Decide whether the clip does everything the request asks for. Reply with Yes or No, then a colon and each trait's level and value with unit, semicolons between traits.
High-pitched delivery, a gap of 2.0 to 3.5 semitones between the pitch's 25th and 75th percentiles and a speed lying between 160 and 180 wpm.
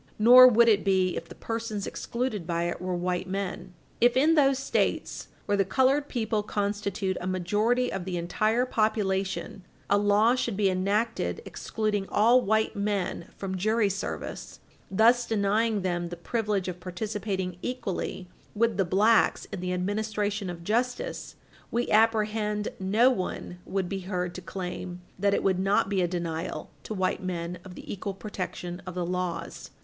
Yes: high, 200 Hz; average, 3.2 semitones; average, 165 wpm